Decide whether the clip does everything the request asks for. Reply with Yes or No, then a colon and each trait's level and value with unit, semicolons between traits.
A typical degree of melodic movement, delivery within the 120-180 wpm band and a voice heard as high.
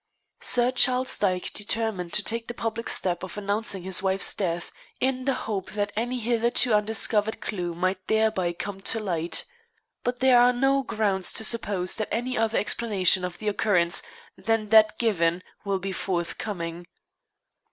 Yes: average, 3.7 semitones; average, 160 wpm; high, 210 Hz